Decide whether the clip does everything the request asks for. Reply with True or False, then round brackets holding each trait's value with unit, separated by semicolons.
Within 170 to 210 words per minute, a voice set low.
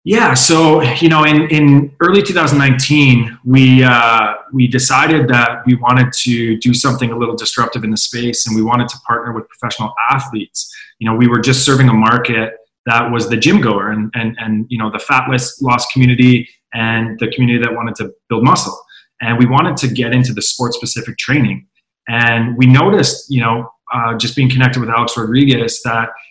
True (195 wpm; 120 Hz)